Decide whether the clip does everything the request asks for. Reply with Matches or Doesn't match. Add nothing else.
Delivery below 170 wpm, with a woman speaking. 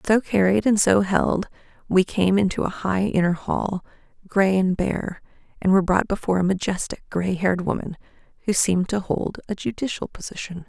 Doesn't match